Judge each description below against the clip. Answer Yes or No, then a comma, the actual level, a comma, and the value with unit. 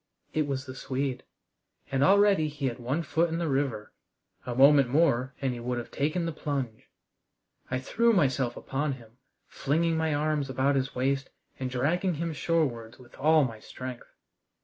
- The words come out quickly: No, average, 170 wpm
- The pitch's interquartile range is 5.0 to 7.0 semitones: No, average, 3.5 semitones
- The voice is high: No, medium, 140 Hz